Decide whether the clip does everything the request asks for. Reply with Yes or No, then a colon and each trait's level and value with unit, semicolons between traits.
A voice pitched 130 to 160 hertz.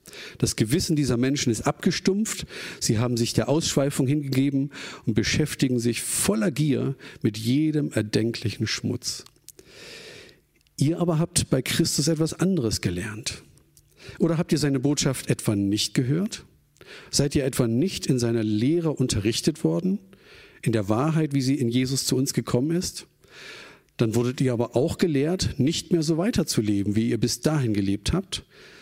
Yes: low, 135 Hz